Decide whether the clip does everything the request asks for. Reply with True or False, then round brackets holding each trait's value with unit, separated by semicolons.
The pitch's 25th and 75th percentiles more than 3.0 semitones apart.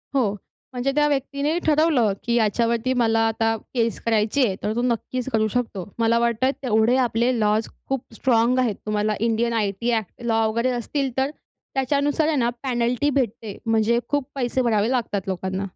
False (2.7 semitones)